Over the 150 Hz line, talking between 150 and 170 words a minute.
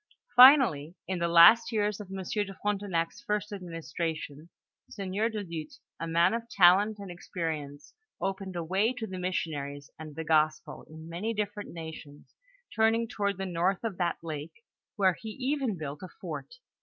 Yes: medium, 185 Hz; average, 165 wpm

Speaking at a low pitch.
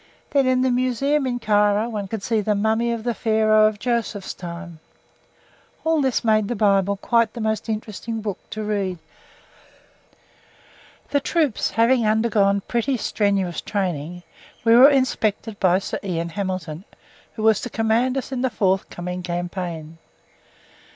No: high, 215 Hz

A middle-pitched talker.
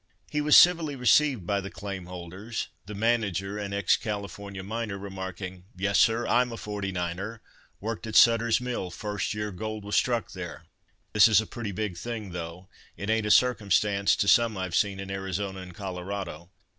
No: low, 100 Hz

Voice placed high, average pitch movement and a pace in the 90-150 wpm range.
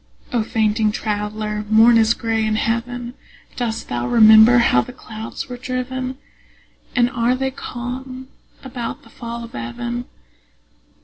No: high, 235 Hz; narrow, 2.2 semitones; slow, 135 wpm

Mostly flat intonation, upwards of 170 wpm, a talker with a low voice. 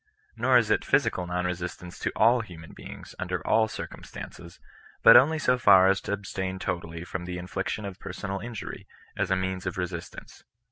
No: average, 3.2 semitones; average, 180 wpm; very low, 95 Hz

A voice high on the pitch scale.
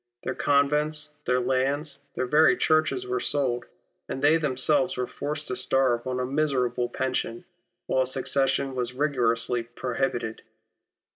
No: low, 130 Hz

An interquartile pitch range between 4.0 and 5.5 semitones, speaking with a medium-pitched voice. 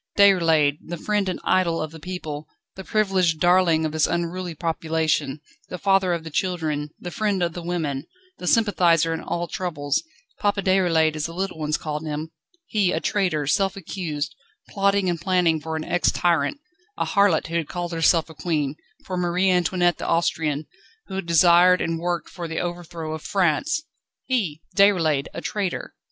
No: average, 2.7 semitones; medium, 170 Hz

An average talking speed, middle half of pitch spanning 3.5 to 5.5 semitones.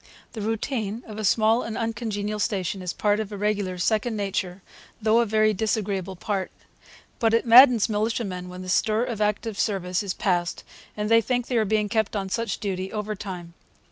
No: average, 185 wpm; narrow, 2.6 semitones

